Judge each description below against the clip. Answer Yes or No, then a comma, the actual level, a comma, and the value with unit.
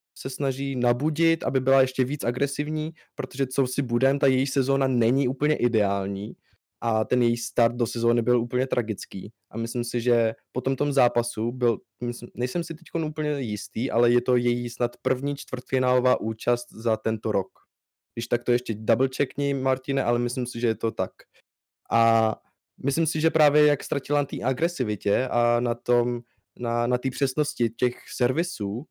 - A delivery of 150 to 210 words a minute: Yes, fast, 170 wpm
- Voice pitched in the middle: No, low, 125 Hz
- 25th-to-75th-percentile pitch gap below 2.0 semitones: No, average, 2.7 semitones